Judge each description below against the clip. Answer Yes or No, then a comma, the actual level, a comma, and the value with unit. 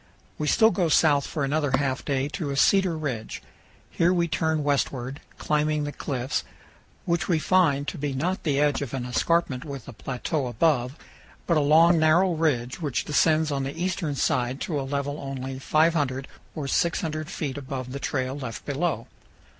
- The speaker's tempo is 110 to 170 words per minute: No, average, 180 wpm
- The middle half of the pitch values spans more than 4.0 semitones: No, average, 3.1 semitones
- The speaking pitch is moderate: Yes, medium, 145 Hz